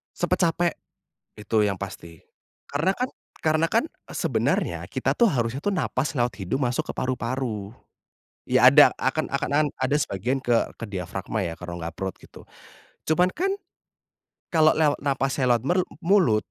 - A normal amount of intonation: No, wide, 7.1 semitones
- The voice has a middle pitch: No, low, 130 Hz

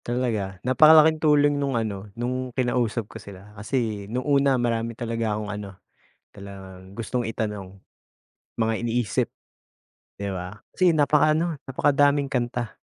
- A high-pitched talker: No, low, 115 Hz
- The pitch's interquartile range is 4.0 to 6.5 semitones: Yes, average, 4.8 semitones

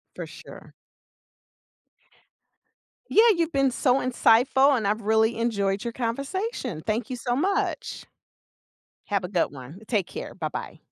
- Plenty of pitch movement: No, average, 5.0 semitones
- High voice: Yes, high, 230 Hz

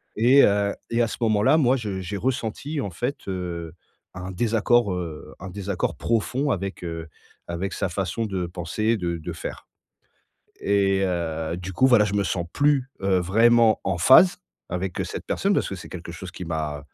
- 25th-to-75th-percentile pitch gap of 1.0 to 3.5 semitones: No, average, 4.7 semitones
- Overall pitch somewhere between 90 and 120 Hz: Yes, very low, 95 Hz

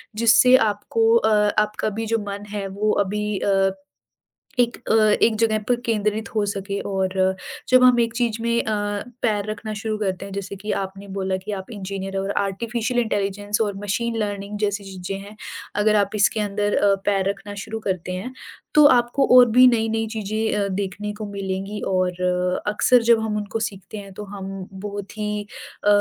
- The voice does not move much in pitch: Yes, narrow, 2.1 semitones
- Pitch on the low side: No, high, 205 Hz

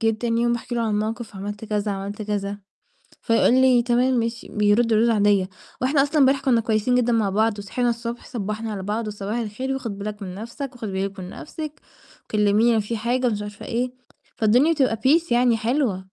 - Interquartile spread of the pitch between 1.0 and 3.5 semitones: Yes, average, 2.9 semitones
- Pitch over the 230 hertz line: No, high, 225 Hz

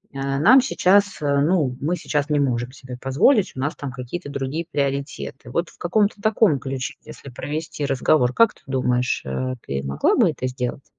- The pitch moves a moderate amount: Yes, average, 4.7 semitones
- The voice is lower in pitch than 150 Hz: Yes, medium, 140 Hz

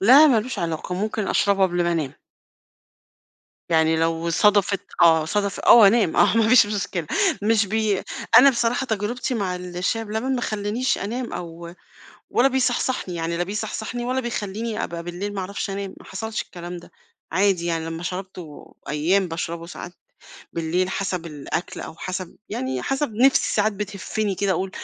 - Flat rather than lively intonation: No, average, 4.2 semitones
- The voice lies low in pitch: No, high, 195 Hz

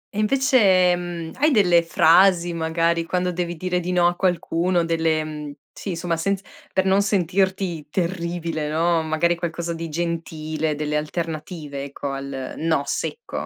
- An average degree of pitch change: No, narrow, 2.3 semitones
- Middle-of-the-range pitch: Yes, medium, 170 Hz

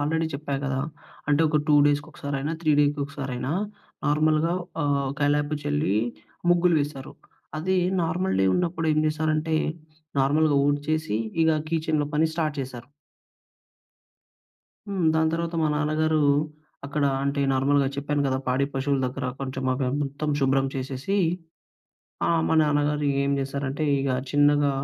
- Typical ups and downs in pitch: No, narrow, 2.2 semitones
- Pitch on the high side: No, medium, 145 Hz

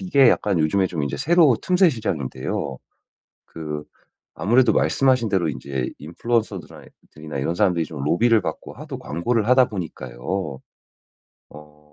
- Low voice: Yes, very low, 90 Hz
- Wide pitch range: Yes, wide, 7.9 semitones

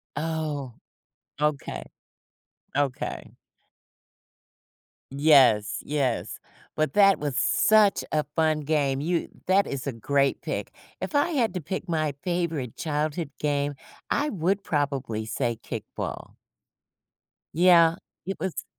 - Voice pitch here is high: No, medium, 150 Hz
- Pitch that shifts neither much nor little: Yes, average, 4.0 semitones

